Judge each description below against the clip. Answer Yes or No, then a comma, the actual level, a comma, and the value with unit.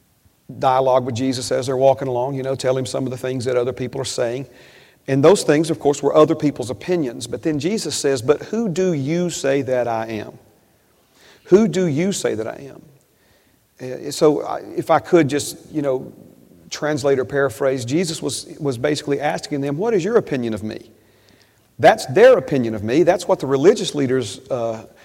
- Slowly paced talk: No, average, 200 wpm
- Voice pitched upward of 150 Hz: No, low, 135 Hz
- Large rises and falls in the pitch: No, average, 3.2 semitones